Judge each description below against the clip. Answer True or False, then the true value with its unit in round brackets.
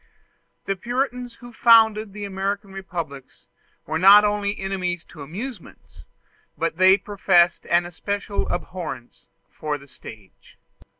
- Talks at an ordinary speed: False (120 wpm)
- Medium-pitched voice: False (195 Hz)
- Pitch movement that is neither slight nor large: True (3.3 semitones)